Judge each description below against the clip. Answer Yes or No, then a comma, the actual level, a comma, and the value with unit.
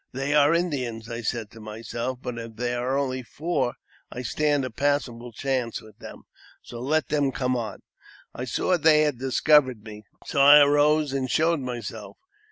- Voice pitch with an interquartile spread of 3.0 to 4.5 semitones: Yes, average, 3.7 semitones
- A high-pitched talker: No, low, 130 Hz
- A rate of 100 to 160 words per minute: No, average, 175 wpm